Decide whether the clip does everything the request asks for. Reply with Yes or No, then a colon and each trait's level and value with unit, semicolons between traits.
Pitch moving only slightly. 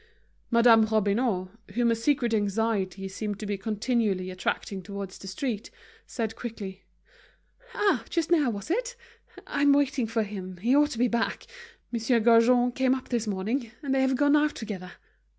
No: average, 4.3 semitones